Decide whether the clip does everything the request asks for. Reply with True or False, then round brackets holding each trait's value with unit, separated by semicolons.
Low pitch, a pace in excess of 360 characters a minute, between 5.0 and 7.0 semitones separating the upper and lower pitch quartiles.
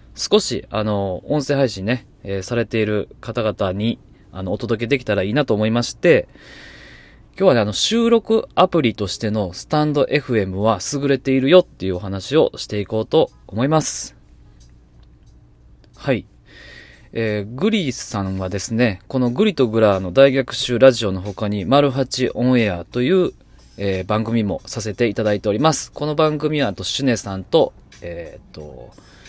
False (110 Hz; 325 characters per minute; 5.5 semitones)